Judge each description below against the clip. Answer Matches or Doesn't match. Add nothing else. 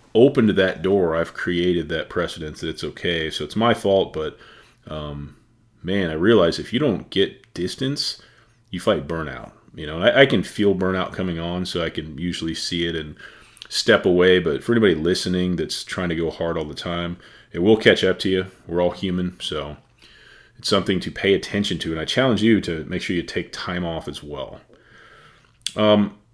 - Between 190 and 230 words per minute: Matches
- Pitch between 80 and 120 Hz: Matches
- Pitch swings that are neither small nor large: Matches